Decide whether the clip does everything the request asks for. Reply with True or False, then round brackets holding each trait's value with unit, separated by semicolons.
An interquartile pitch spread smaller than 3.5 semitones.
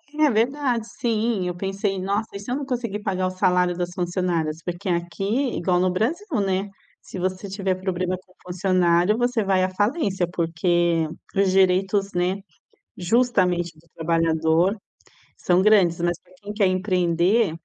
True (2.9 semitones)